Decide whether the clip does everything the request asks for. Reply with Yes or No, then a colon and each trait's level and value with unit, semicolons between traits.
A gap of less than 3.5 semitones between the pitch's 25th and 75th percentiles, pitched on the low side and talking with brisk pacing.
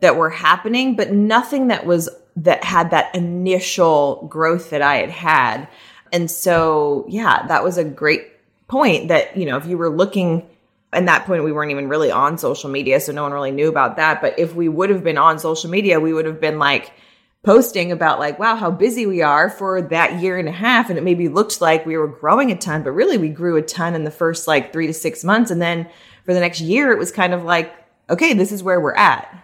No: average, 2.9 semitones; medium, 170 Hz; fast, 240 wpm